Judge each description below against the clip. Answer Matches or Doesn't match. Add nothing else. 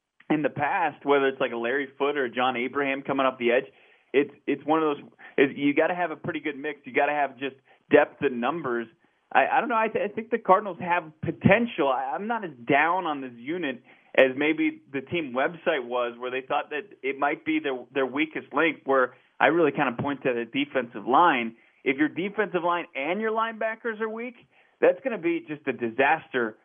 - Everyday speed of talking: Doesn't match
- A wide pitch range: Matches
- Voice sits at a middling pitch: Matches